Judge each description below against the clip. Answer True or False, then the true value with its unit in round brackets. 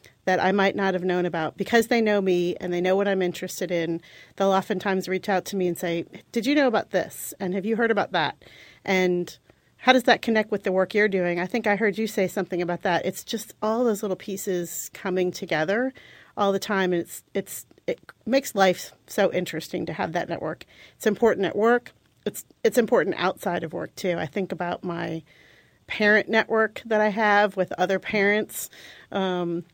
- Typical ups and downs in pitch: True (3.0 semitones)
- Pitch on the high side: True (195 Hz)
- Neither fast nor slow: False (210 wpm)